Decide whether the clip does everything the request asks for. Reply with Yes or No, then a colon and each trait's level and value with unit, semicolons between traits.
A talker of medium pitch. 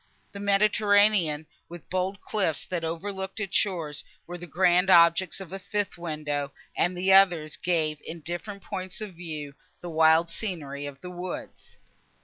Yes: medium, 175 Hz